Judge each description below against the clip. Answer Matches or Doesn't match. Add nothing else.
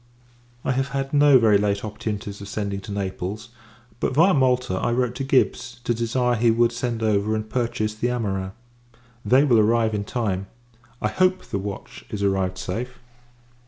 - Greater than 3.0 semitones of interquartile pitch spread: Matches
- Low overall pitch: Matches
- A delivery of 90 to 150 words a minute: Doesn't match